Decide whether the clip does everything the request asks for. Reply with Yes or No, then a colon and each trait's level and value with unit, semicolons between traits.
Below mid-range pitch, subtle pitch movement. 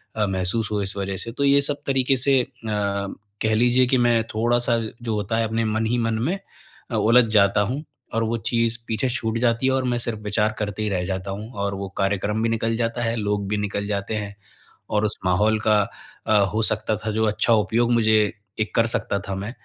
Yes: low, 110 Hz; narrow, 2.3 semitones